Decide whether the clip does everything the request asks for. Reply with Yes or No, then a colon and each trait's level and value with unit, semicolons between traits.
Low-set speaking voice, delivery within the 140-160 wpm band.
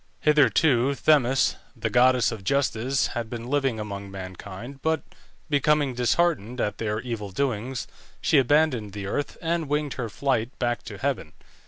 Yes: low, 125 Hz; average, 150 wpm